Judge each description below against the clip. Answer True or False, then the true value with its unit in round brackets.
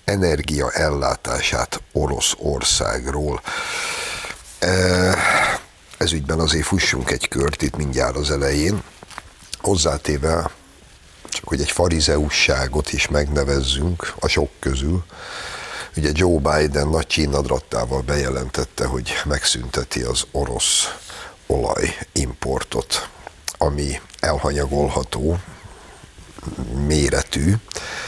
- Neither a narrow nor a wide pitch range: True (3.8 semitones)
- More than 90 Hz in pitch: False (75 Hz)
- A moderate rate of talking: False (80 wpm)